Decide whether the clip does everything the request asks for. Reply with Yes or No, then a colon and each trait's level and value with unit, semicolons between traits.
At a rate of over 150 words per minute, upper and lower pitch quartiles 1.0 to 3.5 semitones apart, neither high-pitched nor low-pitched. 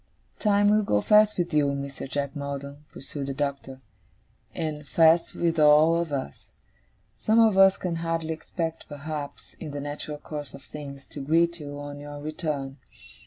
Yes: average, 165 wpm; average, 2.8 semitones; medium, 150 Hz